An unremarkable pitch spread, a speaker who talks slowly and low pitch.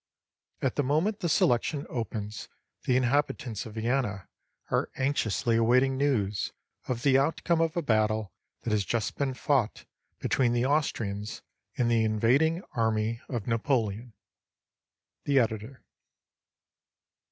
Yes: average, 4.0 semitones; slow, 125 wpm; low, 120 Hz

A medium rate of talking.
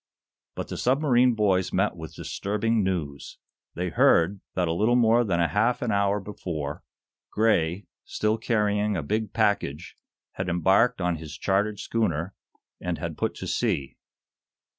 Yes: average, 150 wpm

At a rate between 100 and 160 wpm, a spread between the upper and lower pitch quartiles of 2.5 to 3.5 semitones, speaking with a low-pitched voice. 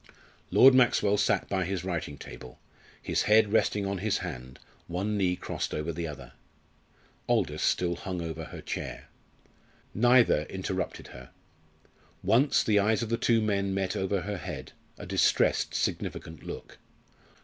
No: average, 150 wpm; average, 3.9 semitones; very low, 95 Hz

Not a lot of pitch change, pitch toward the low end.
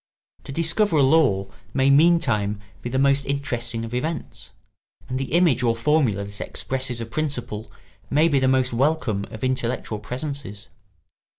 No: average, 4.0 semitones; low, 130 Hz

